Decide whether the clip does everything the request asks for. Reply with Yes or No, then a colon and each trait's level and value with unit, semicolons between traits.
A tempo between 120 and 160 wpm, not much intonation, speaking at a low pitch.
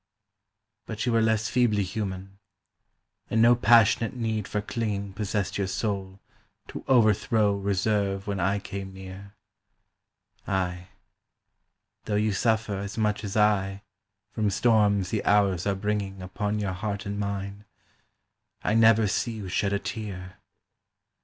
Yes: slow, 135 wpm; narrow, 1.9 semitones; low, 100 Hz